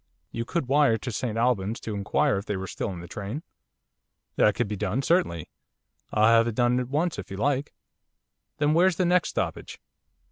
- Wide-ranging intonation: Yes, wide, 5.8 semitones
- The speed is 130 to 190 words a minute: No, average, 200 wpm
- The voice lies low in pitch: Yes, low, 115 Hz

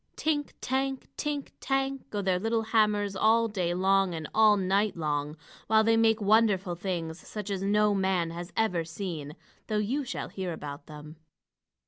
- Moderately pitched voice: No, high, 200 Hz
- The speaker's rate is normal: Yes, average, 165 wpm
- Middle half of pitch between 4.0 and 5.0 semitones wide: Yes, average, 4.3 semitones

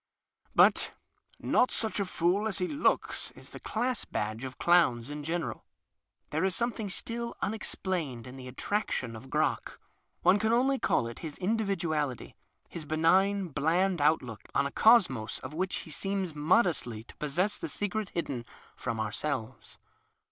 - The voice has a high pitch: No, medium, 170 Hz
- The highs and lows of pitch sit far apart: Yes, wide, 7.0 semitones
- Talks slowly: No, average, 170 wpm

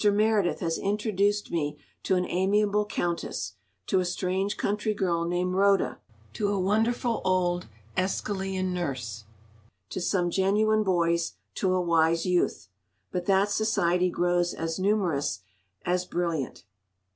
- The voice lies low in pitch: No, medium, 185 Hz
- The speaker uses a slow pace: Yes, slow, 125 wpm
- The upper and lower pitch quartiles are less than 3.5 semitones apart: Yes, average, 2.8 semitones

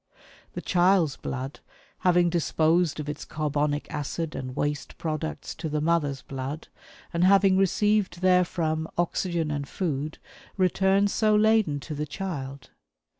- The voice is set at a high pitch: No, medium, 160 Hz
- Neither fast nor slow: No, slow, 130 wpm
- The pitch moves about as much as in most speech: Yes, average, 3.8 semitones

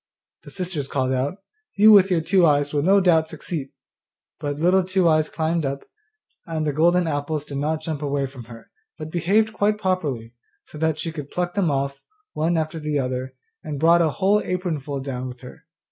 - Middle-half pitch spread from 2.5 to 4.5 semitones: Yes, average, 3.9 semitones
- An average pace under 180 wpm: No, average, 200 wpm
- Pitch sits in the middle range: Yes, medium, 155 Hz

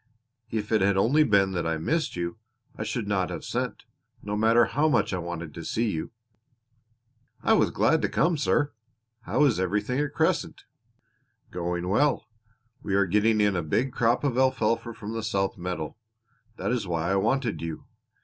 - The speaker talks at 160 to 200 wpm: Yes, average, 180 wpm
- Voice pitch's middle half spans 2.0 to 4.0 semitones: No, average, 5.1 semitones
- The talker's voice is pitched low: Yes, low, 105 Hz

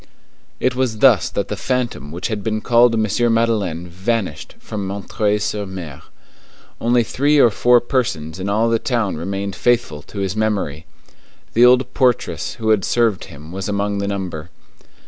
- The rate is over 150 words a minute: Yes, average, 165 wpm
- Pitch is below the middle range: Yes, low, 105 Hz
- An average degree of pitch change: Yes, average, 4.1 semitones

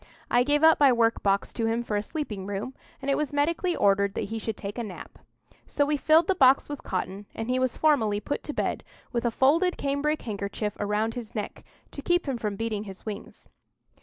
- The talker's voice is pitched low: No, high, 235 Hz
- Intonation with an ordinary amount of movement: No, wide, 5.7 semitones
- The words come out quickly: Yes, fast, 220 wpm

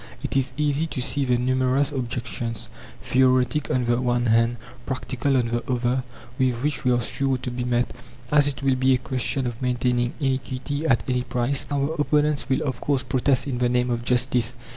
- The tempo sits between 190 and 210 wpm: Yes, average, 195 wpm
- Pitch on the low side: Yes, low, 125 Hz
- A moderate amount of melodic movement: No, narrow, 1.9 semitones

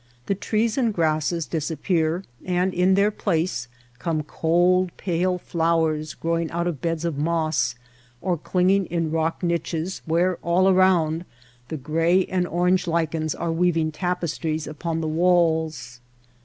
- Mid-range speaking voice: Yes, medium, 170 Hz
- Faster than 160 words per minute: No, average, 140 wpm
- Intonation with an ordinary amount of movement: No, narrow, 2.2 semitones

